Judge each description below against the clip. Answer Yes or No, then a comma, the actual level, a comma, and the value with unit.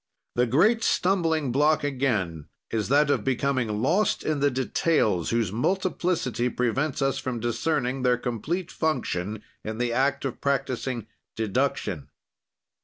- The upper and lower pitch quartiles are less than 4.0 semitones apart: No, average, 4.3 semitones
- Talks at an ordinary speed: No, slow, 130 wpm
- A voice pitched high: No, low, 130 Hz